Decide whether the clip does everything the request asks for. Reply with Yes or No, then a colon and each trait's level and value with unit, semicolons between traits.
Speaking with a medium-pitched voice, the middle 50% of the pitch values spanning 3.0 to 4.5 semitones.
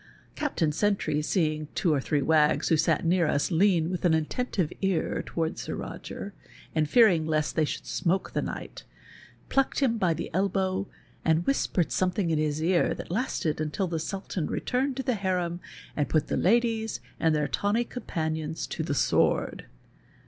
Yes: medium, 170 Hz; average, 4.1 semitones